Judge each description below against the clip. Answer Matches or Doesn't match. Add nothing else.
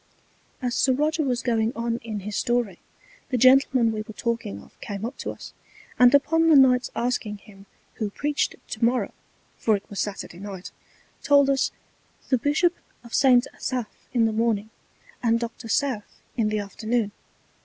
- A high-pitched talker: Matches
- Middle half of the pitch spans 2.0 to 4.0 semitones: Matches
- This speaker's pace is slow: Doesn't match